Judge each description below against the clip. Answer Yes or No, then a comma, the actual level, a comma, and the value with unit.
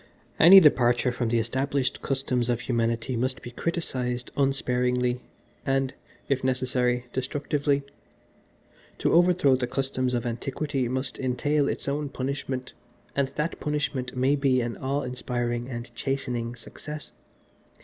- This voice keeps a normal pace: No, slow, 130 wpm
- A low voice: Yes, low, 130 Hz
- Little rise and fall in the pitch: Yes, narrow, 2.2 semitones